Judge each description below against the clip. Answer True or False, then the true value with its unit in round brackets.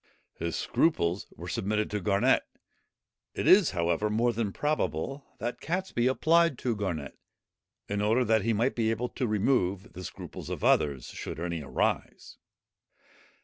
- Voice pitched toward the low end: True (105 Hz)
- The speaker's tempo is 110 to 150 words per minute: True (145 wpm)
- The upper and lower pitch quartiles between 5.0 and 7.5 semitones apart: True (5.3 semitones)